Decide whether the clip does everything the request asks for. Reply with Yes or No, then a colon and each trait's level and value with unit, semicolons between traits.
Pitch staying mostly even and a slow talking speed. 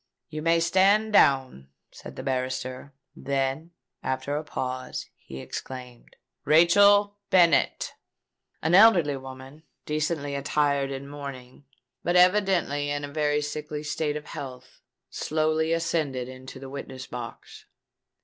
No: average, 3.7 semitones; slow, 120 wpm